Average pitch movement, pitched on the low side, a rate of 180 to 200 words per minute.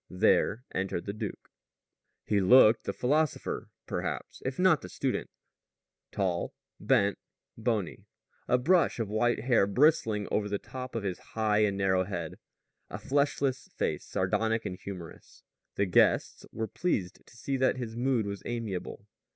No: average, 4.4 semitones; low, 110 Hz; average, 150 wpm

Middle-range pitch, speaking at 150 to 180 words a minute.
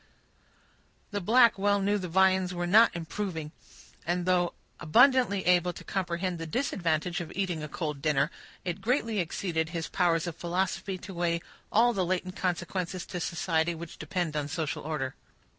Yes: medium, 180 Hz; average, 160 wpm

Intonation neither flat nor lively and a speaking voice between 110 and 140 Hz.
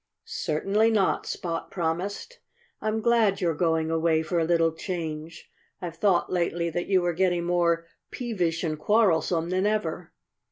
No: average, 3.1 semitones; medium, 175 Hz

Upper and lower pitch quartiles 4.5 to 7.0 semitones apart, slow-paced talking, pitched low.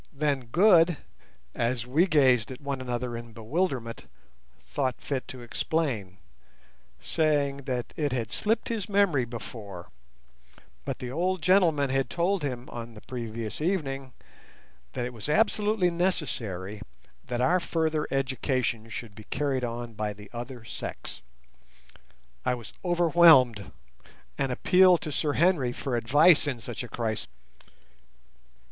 Yes: wide, 5.5 semitones; slow, 130 wpm; low, 130 Hz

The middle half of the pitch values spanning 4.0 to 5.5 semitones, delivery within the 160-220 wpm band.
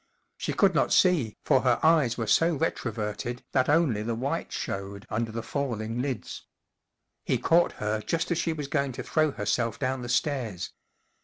Yes: average, 5.2 semitones; average, 175 wpm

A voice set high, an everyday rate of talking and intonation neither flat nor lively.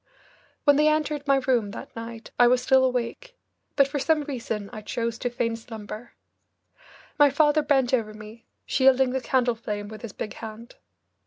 Yes: high, 245 Hz; average, 175 wpm; average, 3.5 semitones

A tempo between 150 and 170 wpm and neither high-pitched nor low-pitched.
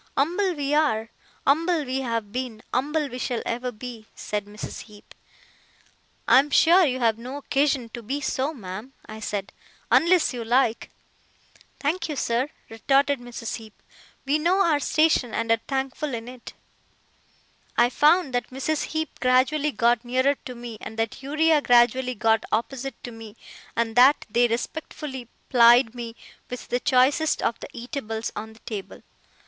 No: average, 160 wpm; very high, 250 Hz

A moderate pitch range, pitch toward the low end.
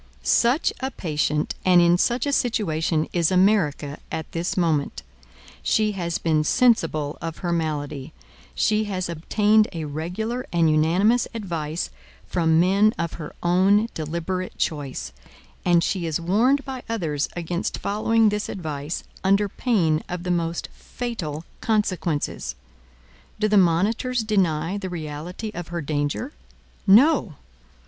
No: average, 4.9 semitones; medium, 175 Hz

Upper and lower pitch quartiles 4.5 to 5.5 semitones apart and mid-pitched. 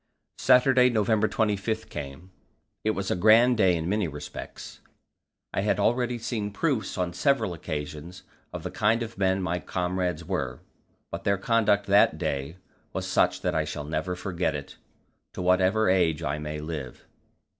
No: average, 5.1 semitones; very low, 95 Hz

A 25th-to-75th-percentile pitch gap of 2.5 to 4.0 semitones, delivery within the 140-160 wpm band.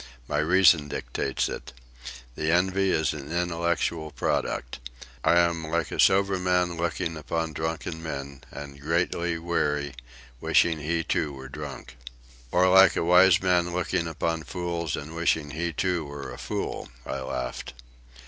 Yes: average, 3.0 semitones; average, 150 wpm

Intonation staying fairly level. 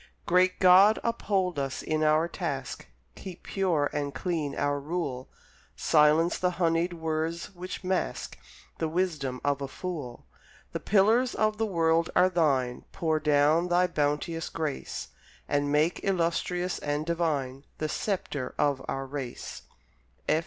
No: average, 3.9 semitones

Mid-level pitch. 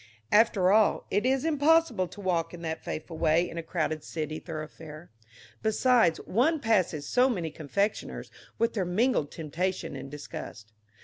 Yes: medium, 180 Hz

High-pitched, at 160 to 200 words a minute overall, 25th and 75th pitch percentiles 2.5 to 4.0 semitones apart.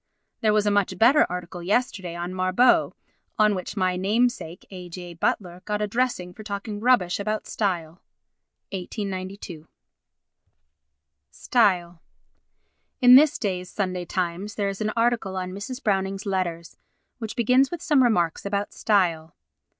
No: high, 195 Hz; average, 140 wpm; average, 3.2 semitones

